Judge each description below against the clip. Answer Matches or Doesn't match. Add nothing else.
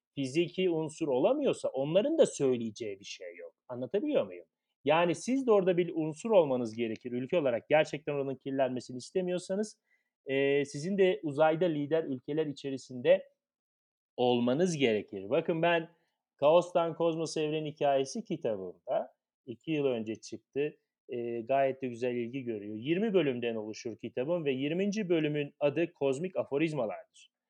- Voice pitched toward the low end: Doesn't match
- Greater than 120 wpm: Matches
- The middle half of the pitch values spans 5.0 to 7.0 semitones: Matches